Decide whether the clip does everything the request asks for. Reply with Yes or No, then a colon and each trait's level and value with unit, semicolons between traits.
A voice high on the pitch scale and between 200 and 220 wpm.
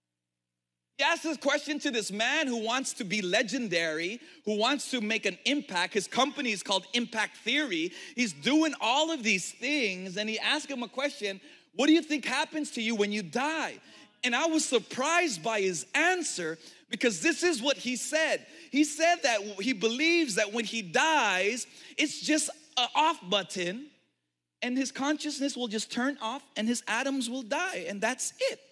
No: very high, 250 Hz; average, 185 wpm